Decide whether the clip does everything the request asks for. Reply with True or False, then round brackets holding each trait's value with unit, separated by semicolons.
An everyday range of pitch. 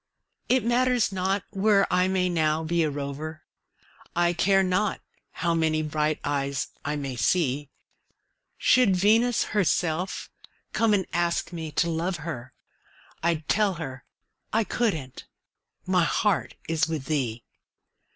True (4.1 semitones)